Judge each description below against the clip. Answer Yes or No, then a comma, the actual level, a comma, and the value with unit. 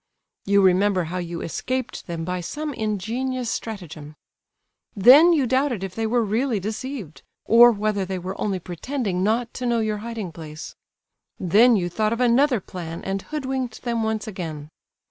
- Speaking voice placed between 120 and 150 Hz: No, high, 215 Hz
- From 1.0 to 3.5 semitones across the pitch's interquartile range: No, average, 5.0 semitones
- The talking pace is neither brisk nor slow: Yes, average, 165 wpm